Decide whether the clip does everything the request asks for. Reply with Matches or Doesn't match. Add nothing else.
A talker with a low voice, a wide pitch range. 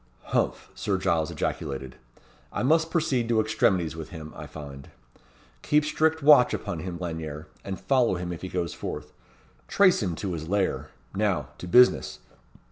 Matches